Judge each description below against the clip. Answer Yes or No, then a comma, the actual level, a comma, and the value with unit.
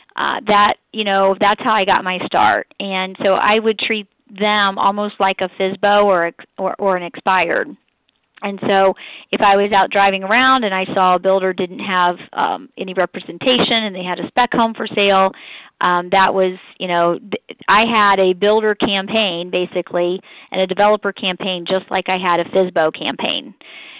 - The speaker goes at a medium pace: Yes, average, 185 wpm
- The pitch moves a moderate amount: No, narrow, 1.9 semitones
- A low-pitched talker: No, high, 195 Hz